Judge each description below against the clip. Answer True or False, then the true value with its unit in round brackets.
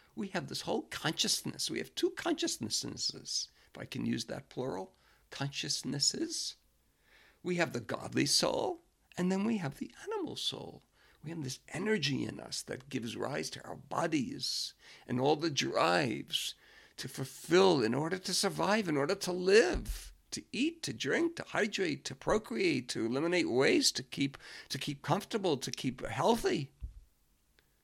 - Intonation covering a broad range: True (9.0 semitones)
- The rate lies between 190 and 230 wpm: False (155 wpm)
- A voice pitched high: False (170 Hz)